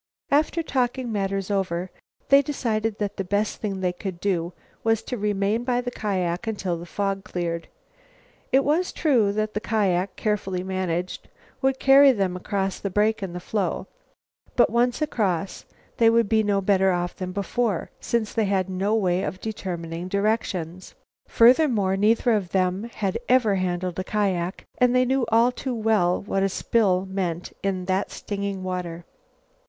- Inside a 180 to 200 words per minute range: No, average, 165 wpm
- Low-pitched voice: No, high, 200 Hz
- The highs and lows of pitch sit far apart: No, average, 3.5 semitones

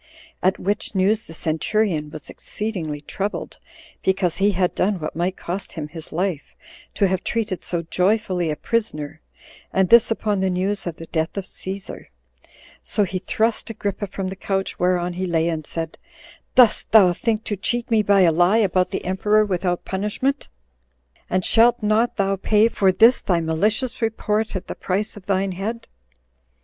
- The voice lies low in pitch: No, high, 190 Hz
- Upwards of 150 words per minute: Yes, average, 175 wpm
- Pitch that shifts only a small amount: No, average, 3.2 semitones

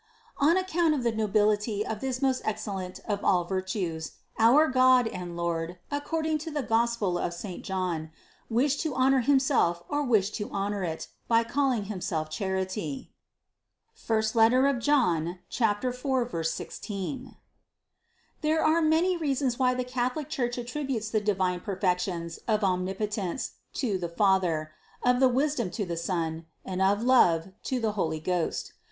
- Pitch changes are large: Yes, wide, 6.0 semitones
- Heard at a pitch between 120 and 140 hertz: No, high, 220 Hz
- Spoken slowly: No, average, 150 wpm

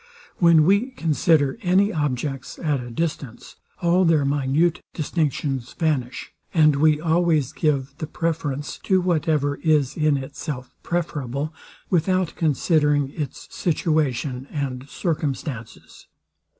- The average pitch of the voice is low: No, medium, 150 Hz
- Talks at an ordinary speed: No, slow, 110 wpm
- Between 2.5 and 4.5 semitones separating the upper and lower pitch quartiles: Yes, average, 3.2 semitones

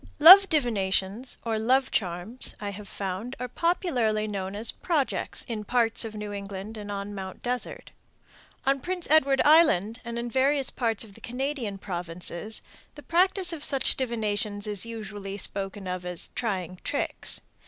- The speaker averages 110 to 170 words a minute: Yes, average, 155 wpm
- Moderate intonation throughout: Yes, average, 5.0 semitones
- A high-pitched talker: Yes, high, 220 Hz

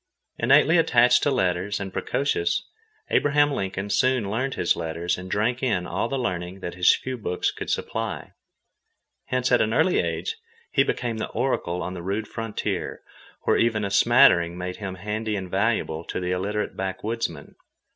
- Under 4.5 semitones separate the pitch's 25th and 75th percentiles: No, average, 5.2 semitones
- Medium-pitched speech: No, low, 105 Hz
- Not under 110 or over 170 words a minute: Yes, average, 165 wpm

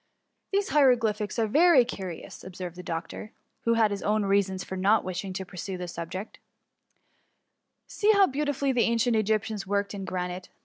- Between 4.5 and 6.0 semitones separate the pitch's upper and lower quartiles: No, average, 3.9 semitones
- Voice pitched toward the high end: Yes, high, 205 Hz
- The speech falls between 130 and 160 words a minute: No, average, 180 wpm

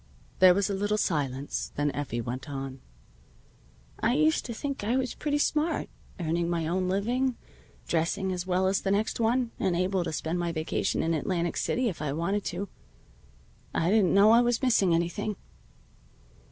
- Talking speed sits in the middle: Yes, average, 180 wpm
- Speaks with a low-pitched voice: No, medium, 185 Hz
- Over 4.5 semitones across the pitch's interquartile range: Yes, average, 5.0 semitones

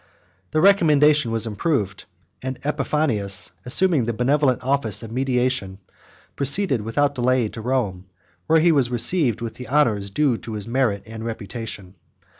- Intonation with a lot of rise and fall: No, average, 4.5 semitones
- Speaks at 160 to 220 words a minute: No, average, 145 wpm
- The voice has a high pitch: No, low, 125 Hz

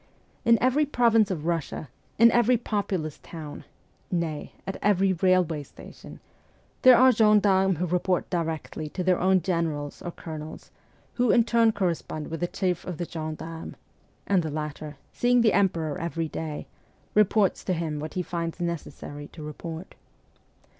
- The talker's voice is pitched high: No, medium, 175 Hz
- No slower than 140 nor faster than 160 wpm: Yes, average, 155 wpm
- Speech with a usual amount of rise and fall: Yes, average, 4.3 semitones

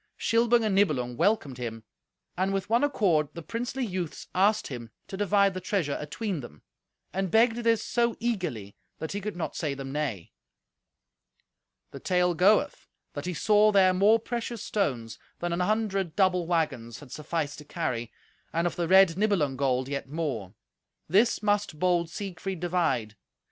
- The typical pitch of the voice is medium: Yes, medium, 180 Hz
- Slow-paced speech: No, average, 165 wpm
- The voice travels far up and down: Yes, wide, 5.9 semitones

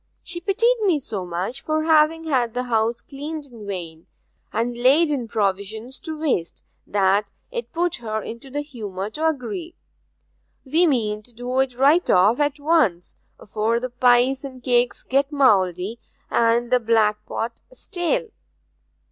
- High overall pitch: Yes, very high, 250 Hz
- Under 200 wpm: Yes, average, 150 wpm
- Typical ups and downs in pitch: No, wide, 5.7 semitones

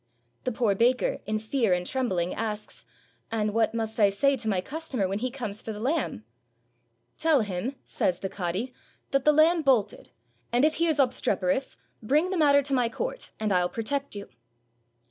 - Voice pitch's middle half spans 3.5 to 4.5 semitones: No, average, 5.2 semitones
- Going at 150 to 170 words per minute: No, average, 185 wpm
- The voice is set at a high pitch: Yes, high, 230 Hz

